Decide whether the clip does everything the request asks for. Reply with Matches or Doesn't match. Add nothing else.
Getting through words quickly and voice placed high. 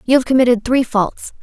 Matches